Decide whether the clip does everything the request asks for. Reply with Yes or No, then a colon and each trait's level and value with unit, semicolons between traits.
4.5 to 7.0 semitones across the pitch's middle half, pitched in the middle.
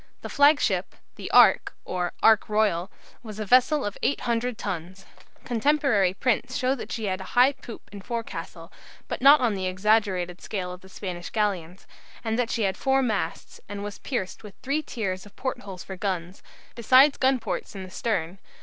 No: average, 4.9 semitones; high, 210 Hz